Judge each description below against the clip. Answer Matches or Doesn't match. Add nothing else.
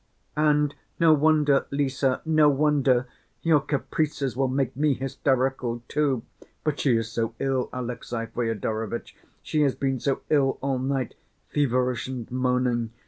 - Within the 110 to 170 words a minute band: Matches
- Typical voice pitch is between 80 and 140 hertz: Matches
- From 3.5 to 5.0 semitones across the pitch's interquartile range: Doesn't match